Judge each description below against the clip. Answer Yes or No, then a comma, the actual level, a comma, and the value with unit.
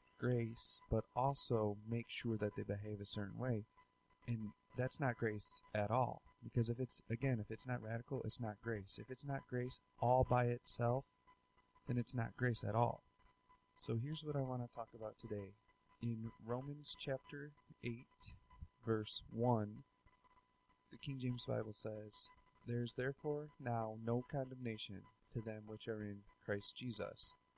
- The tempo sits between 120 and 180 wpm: Yes, average, 160 wpm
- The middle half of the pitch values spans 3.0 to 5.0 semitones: No, narrow, 2.6 semitones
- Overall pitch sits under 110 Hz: No, low, 115 Hz